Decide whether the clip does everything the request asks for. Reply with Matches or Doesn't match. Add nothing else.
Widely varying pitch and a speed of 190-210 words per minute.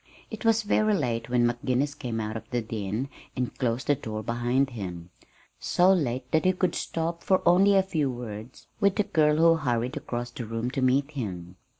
Matches